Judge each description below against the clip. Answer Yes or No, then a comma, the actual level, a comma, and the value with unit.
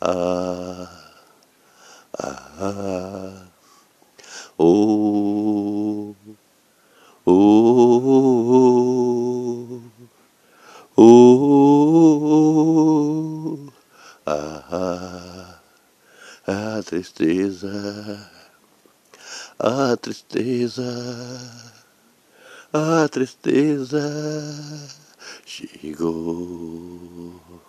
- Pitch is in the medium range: No, low, 115 Hz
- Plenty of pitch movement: Yes, wide, 6.3 semitones